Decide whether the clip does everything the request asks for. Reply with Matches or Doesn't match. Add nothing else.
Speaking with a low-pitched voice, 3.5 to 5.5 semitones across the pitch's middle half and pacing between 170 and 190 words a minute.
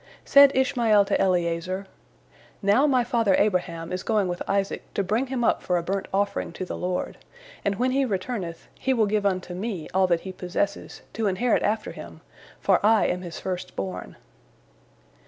Doesn't match